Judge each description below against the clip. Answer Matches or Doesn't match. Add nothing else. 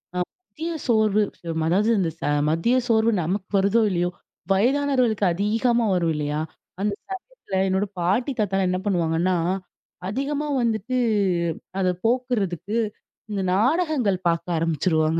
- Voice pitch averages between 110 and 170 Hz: Doesn't match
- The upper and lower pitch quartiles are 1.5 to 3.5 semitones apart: Doesn't match